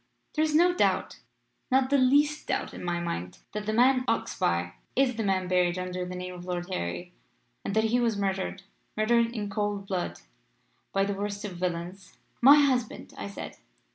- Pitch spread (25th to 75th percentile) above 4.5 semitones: Yes, average, 5.1 semitones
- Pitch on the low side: No, high, 200 Hz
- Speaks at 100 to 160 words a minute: No, average, 190 wpm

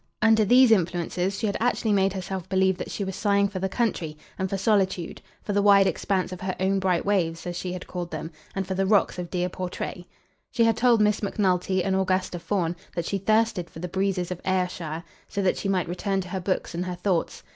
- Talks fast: Yes, fast, 230 wpm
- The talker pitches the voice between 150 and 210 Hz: Yes, high, 190 Hz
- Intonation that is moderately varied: No, narrow, 2.0 semitones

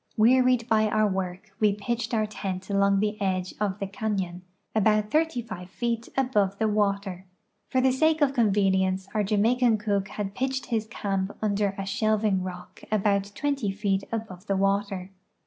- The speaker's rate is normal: Yes, average, 165 wpm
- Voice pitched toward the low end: No, high, 205 Hz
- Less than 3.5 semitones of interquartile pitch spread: Yes, narrow, 2.5 semitones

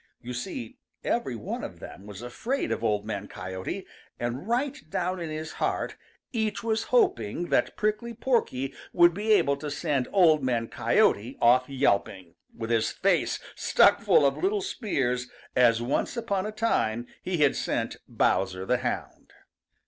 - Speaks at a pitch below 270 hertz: Yes, medium, 140 Hz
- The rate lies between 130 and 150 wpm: No, average, 160 wpm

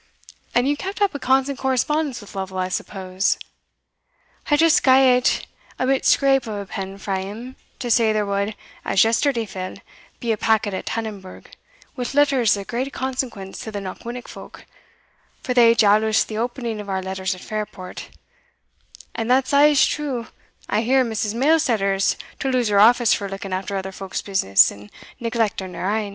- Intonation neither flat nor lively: Yes, average, 4.8 semitones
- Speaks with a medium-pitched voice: No, high, 225 Hz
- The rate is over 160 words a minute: Yes, average, 175 wpm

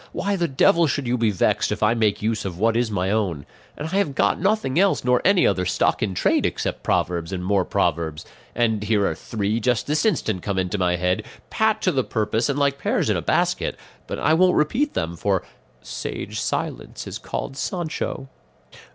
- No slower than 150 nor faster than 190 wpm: No, fast, 205 wpm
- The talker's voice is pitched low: Yes, low, 115 Hz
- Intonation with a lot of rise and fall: Yes, wide, 7.5 semitones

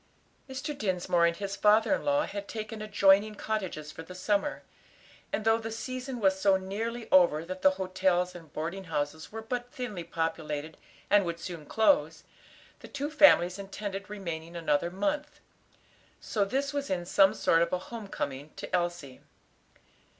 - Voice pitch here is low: No, high, 195 Hz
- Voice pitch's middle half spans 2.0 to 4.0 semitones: No, average, 4.4 semitones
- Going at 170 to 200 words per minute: No, average, 160 wpm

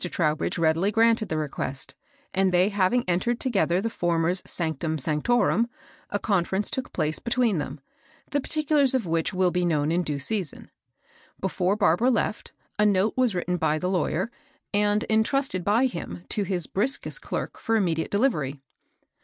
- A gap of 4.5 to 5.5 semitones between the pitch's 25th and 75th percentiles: Yes, average, 5.2 semitones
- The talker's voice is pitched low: No, high, 190 Hz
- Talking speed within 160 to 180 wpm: Yes, average, 170 wpm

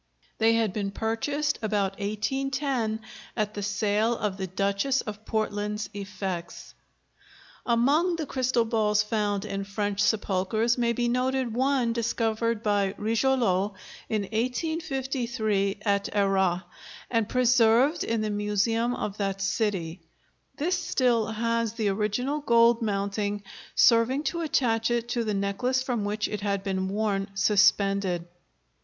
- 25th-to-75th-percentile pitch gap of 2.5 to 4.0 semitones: Yes, average, 3.0 semitones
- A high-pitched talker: Yes, high, 220 Hz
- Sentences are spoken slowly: Yes, slow, 130 wpm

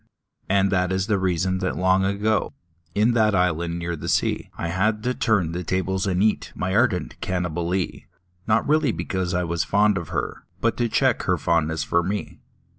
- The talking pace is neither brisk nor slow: Yes, average, 190 wpm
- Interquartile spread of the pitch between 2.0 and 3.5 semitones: Yes, average, 3.1 semitones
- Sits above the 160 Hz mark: No, very low, 95 Hz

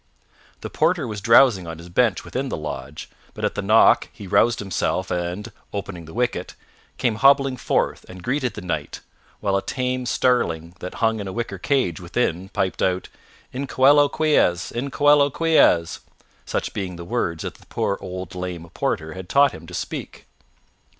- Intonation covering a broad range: Yes, wide, 6.3 semitones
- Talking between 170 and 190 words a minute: Yes, average, 175 wpm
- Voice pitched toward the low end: Yes, low, 100 Hz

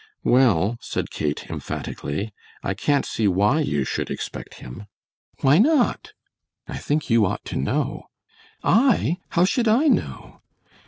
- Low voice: Yes, low, 125 Hz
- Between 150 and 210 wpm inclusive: No, average, 140 wpm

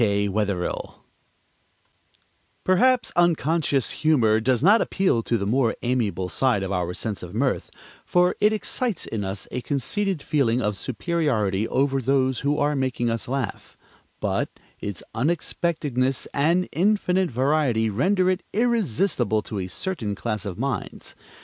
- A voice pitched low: Yes, low, 130 Hz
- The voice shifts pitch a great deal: Yes, wide, 7.7 semitones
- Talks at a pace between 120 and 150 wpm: Yes, average, 140 wpm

